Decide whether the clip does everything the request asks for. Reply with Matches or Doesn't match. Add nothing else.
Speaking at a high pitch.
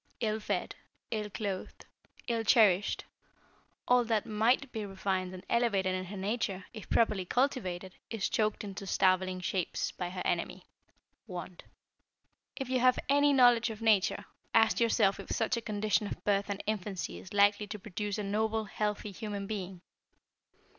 Matches